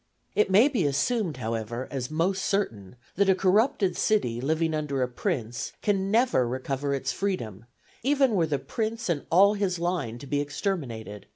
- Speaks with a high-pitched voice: No, medium, 160 Hz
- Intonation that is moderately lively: No, wide, 7.6 semitones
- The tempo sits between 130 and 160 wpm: No, average, 170 wpm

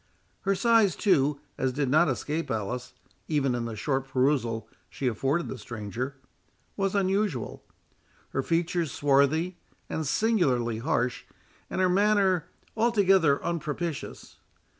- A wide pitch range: Yes, wide, 6.4 semitones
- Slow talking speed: Yes, slow, 120 wpm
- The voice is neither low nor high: Yes, medium, 150 Hz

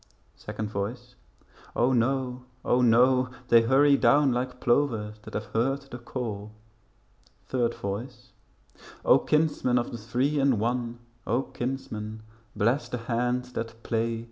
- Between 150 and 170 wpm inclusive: No, slow, 135 wpm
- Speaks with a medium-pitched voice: No, low, 120 Hz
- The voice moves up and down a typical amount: No, narrow, 2.1 semitones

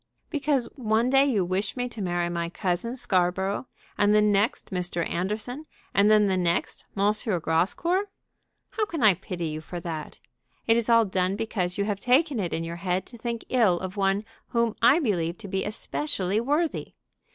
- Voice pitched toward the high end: Yes, high, 205 Hz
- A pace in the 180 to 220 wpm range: Yes, average, 185 wpm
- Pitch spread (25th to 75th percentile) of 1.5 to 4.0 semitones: No, average, 4.6 semitones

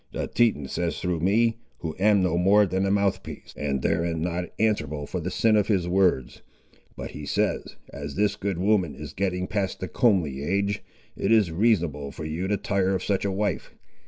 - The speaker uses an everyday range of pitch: Yes, average, 3.6 semitones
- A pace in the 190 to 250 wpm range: Yes, average, 195 wpm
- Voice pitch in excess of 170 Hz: No, very low, 95 Hz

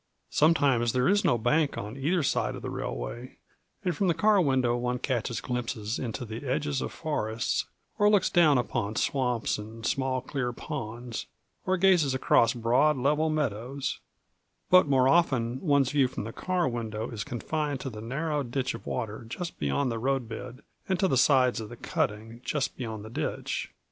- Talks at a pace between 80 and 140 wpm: No, average, 180 wpm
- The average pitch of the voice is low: Yes, low, 130 Hz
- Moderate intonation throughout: Yes, average, 4.3 semitones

